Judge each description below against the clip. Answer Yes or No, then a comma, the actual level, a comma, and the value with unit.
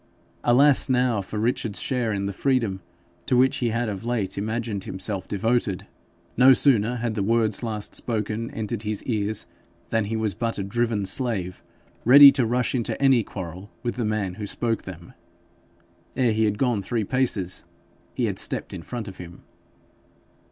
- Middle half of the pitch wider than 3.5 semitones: No, average, 3.2 semitones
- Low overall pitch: Yes, low, 110 Hz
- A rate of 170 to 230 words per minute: Yes, average, 175 wpm